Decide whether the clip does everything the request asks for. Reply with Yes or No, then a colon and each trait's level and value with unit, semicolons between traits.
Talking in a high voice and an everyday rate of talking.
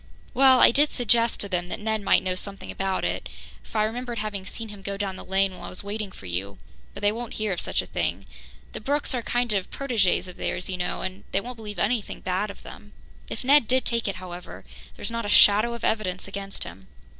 No: high, 205 Hz; fast, 240 wpm